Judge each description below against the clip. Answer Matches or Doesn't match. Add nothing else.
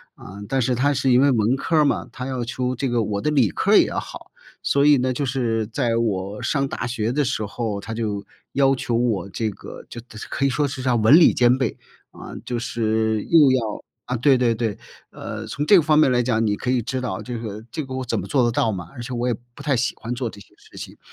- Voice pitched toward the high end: Doesn't match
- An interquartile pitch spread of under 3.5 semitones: Matches